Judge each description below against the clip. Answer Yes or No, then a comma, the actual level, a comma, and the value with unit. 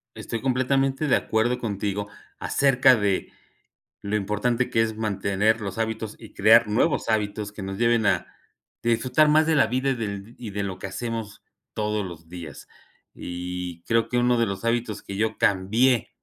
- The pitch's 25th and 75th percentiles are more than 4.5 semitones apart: No, average, 3.2 semitones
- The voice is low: Yes, low, 110 Hz